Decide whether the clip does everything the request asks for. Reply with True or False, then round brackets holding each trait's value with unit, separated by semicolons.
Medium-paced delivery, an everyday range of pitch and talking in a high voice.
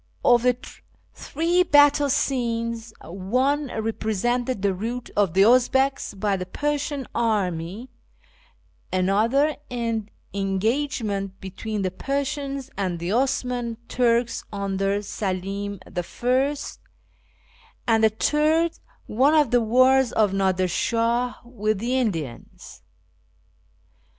False (105 wpm; 4.9 semitones; 230 Hz)